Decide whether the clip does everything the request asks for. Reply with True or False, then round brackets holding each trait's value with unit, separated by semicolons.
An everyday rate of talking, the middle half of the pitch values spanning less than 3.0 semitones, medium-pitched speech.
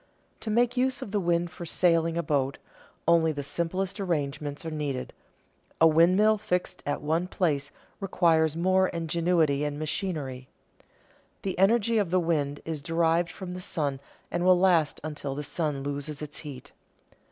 False (160 wpm; 3.6 semitones; 165 Hz)